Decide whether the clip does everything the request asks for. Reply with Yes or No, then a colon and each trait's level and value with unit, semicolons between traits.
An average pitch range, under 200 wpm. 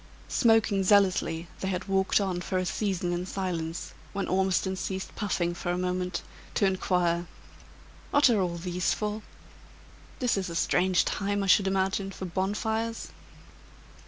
No: narrow, 2.0 semitones; average, 150 wpm